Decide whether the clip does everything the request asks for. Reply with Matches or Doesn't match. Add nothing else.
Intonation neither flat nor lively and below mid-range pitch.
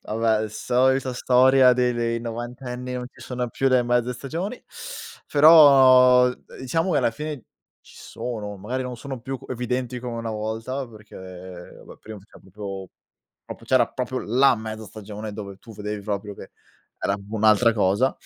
Matches